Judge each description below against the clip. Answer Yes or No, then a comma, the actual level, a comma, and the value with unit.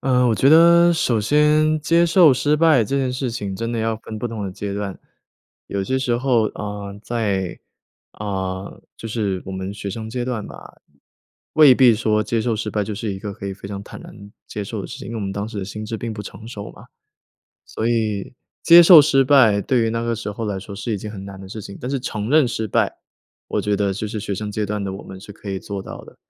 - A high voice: No, low, 110 Hz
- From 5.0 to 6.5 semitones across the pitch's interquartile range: No, average, 3.8 semitones